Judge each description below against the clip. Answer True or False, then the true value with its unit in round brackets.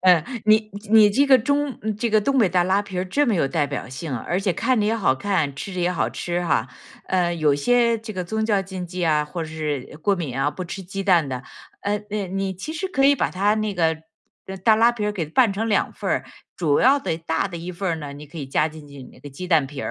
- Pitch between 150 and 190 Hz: True (185 Hz)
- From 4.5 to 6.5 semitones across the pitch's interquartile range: True (5.1 semitones)